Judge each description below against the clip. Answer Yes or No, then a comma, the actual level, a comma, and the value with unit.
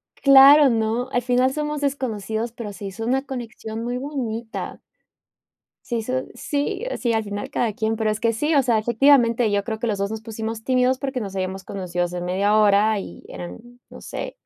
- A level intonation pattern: No, average, 3.5 semitones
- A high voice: Yes, high, 225 Hz